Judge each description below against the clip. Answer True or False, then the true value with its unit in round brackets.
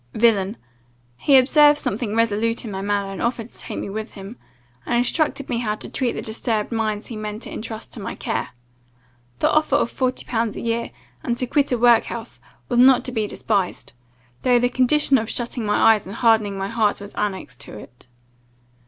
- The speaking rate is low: False (200 wpm)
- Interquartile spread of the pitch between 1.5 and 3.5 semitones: True (2.8 semitones)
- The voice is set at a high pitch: True (230 Hz)